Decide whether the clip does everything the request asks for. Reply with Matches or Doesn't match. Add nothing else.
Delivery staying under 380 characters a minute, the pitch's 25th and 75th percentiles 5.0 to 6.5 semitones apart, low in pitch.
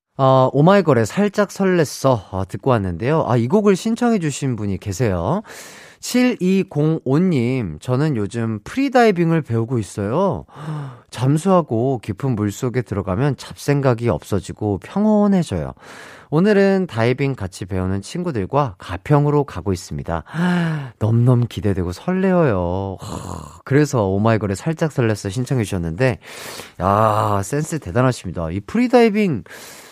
Doesn't match